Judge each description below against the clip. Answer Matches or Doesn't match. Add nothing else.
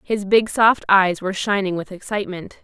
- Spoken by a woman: Matches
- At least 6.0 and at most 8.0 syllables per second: Doesn't match